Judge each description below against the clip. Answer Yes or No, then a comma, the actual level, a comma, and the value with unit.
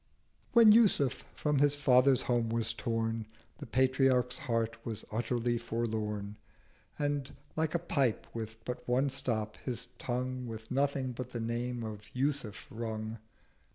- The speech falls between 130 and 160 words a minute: Yes, average, 145 wpm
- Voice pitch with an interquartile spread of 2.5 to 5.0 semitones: Yes, average, 2.9 semitones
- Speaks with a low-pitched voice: Yes, low, 120 Hz